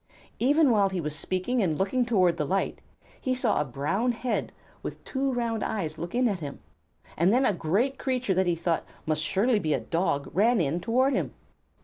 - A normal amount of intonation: No, wide, 6.8 semitones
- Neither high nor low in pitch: No, high, 195 Hz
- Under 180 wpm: No, fast, 205 wpm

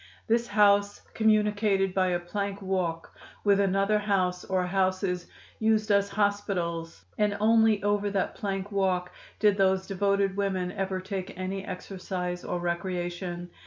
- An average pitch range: No, narrow, 1.9 semitones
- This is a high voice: Yes, high, 195 Hz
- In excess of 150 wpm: No, slow, 135 wpm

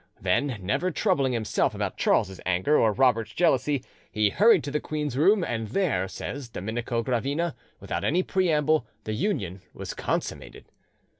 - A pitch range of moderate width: No, wide, 6.3 semitones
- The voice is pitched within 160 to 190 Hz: No, low, 130 Hz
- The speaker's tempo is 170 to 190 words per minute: No, average, 150 wpm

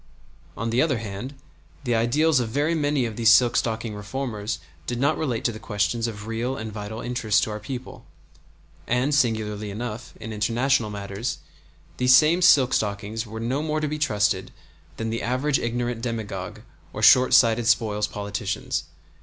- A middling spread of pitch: Yes, average, 3.2 semitones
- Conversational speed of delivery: Yes, average, 165 wpm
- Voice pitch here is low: Yes, low, 115 Hz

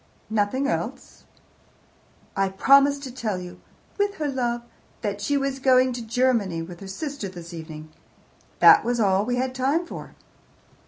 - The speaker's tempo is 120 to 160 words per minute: Yes, average, 155 wpm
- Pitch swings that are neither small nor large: No, wide, 5.8 semitones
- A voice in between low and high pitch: No, high, 240 Hz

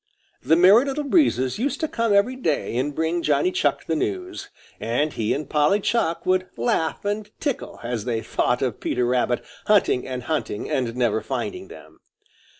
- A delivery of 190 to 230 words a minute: No, average, 175 wpm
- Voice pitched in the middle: Yes, medium, 160 Hz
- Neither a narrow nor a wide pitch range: No, wide, 9.0 semitones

